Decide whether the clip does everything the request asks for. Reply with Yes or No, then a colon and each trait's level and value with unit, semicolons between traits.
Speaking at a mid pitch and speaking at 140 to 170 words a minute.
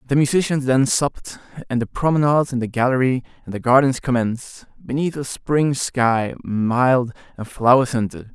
No: low, 130 Hz; average, 160 wpm